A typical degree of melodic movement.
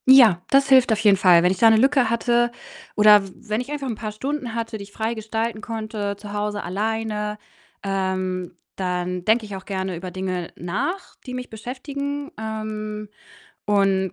Yes: average, 3.5 semitones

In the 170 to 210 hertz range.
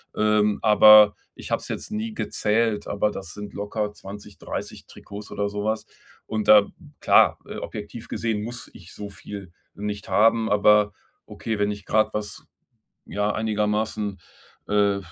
No: low, 105 Hz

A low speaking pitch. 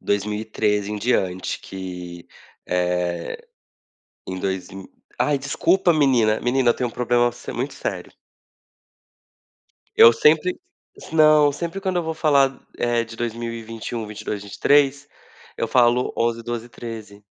Yes: low, 115 Hz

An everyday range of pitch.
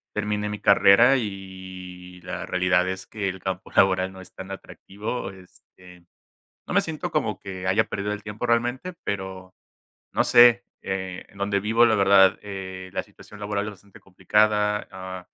No: narrow, 1.9 semitones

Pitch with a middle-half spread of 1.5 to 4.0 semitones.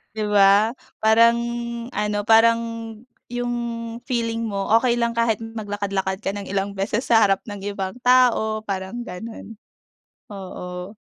Yes: average, 2.7 semitones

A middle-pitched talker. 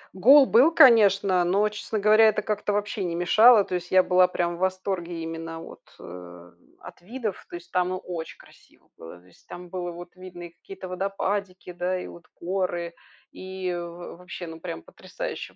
Yes: medium, 180 Hz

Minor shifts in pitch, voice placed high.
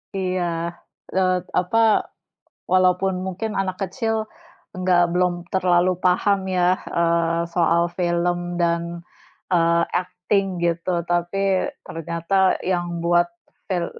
No: narrow, 1.5 semitones; medium, 180 Hz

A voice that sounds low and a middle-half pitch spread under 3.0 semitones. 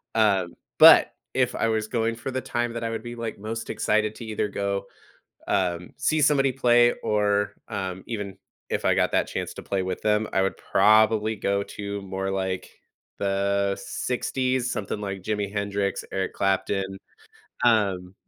Yes: low, 105 Hz; narrow, 2.6 semitones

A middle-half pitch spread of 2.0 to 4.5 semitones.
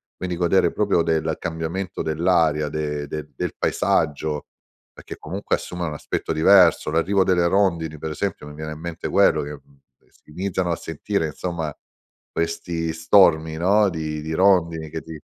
Yes: narrow, 2.5 semitones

